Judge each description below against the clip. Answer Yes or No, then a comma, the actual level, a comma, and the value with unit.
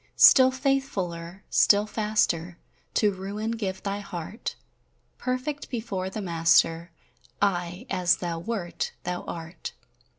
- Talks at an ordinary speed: No, slow, 110 wpm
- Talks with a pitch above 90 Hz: Yes, high, 190 Hz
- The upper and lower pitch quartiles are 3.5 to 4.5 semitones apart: Yes, average, 4.1 semitones